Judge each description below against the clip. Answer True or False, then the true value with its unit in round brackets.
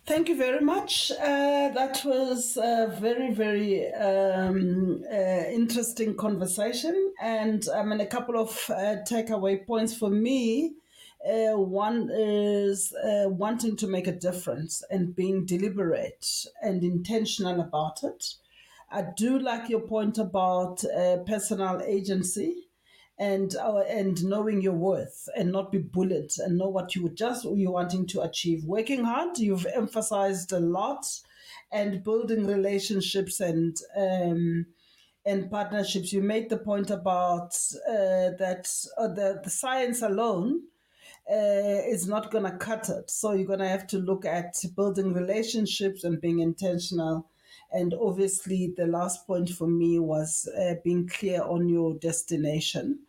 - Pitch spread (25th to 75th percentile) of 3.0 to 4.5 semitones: True (3.5 semitones)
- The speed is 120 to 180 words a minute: True (145 wpm)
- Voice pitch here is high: True (200 Hz)